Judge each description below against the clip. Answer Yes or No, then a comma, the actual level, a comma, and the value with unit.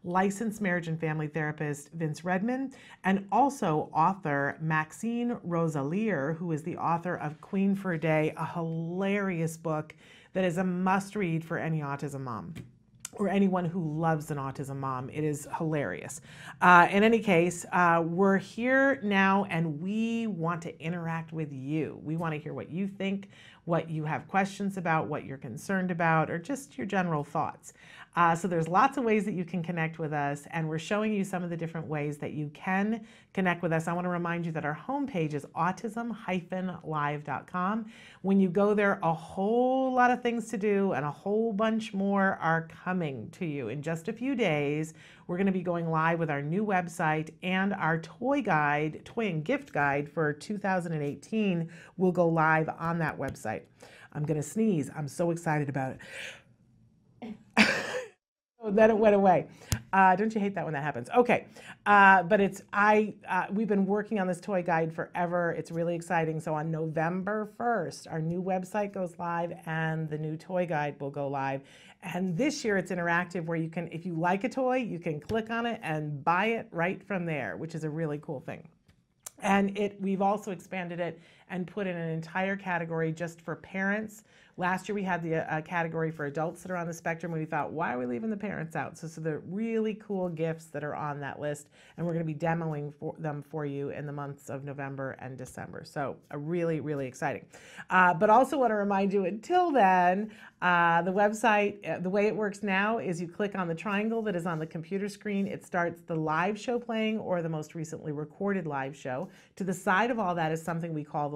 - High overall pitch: No, medium, 175 Hz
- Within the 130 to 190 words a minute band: No, fast, 205 wpm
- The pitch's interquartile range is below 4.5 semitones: Yes, average, 4.0 semitones